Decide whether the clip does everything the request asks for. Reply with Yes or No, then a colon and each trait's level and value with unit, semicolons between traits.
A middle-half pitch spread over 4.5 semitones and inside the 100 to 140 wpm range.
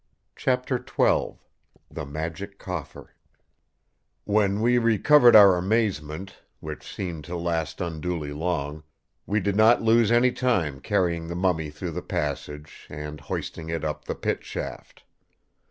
Yes: average, 5.2 semitones; slow, 135 wpm